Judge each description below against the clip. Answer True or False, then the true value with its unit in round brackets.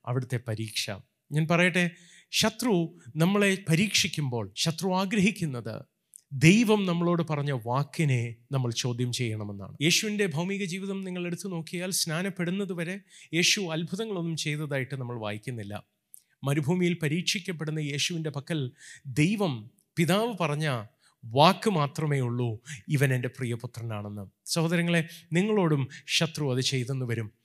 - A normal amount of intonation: False (5.8 semitones)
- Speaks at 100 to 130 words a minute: True (105 wpm)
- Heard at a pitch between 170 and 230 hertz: False (155 Hz)